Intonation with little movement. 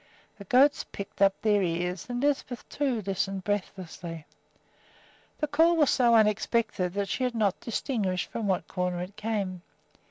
No: average, 4.7 semitones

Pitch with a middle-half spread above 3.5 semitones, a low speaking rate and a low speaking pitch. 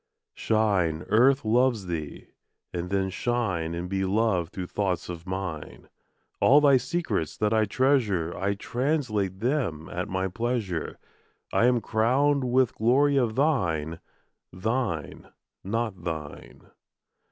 Yes: wide, 5.6 semitones; slow, 125 wpm; low, 105 Hz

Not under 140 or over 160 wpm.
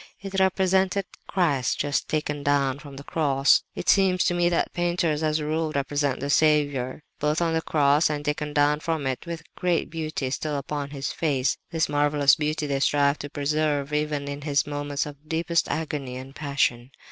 No: average, 185 wpm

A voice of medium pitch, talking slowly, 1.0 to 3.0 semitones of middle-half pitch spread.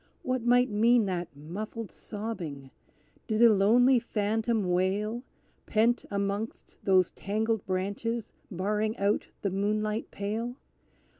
No: high, 210 Hz; slow, 115 wpm; narrow, 2.6 semitones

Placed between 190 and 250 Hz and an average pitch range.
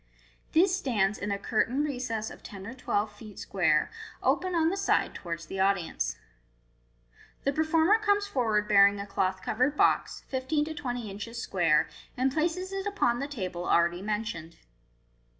No: high, 225 Hz; wide, 7.4 semitones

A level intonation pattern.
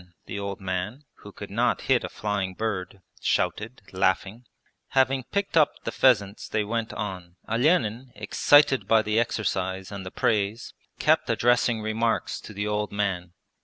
No: average, 3.3 semitones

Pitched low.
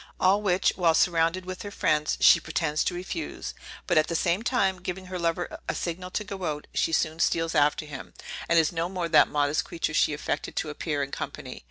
No: medium, 170 Hz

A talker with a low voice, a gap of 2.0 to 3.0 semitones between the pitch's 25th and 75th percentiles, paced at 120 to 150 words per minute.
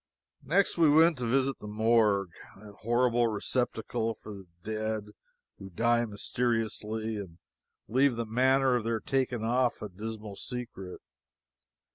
Yes: low, 115 Hz; average, 2.7 semitones; slow, 135 wpm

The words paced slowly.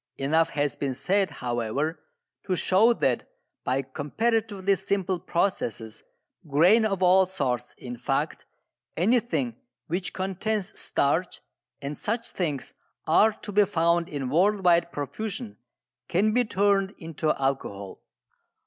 Yes: slow, 120 wpm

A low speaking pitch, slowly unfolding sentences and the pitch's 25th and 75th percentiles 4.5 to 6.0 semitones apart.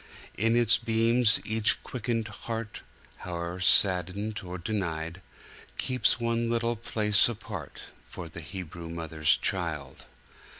Yes: low, 105 Hz; slow, 110 wpm; average, 5.1 semitones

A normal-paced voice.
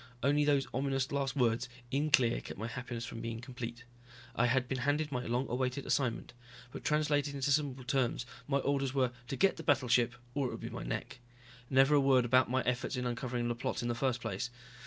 No: fast, 215 wpm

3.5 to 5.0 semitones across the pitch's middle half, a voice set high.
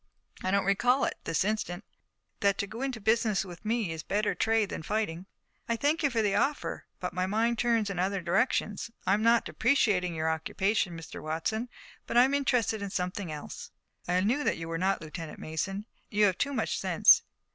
Yes: average, 4.2 semitones; high, 200 Hz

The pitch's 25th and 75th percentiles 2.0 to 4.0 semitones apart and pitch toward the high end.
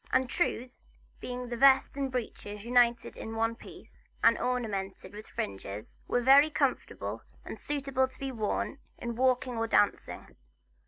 Yes: average, 2.7 semitones; high, 245 Hz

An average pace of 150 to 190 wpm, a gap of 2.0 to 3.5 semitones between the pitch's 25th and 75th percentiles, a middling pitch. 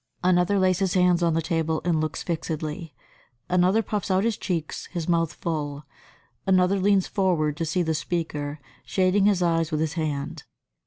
Yes: average, 170 wpm; average, 2.8 semitones; medium, 170 Hz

